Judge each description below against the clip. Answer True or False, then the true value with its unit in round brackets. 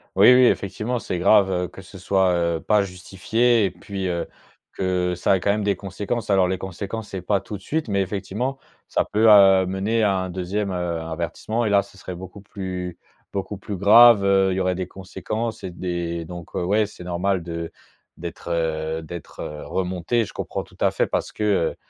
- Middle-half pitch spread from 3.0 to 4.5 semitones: False (2.6 semitones)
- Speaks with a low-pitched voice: True (95 Hz)